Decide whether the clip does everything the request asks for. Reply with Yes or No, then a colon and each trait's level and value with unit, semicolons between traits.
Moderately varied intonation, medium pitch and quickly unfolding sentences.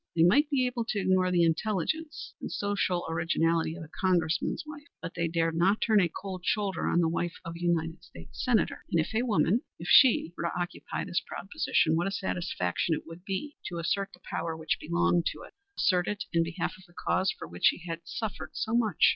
Yes: average, 3.7 semitones; medium, 175 Hz; fast, 220 wpm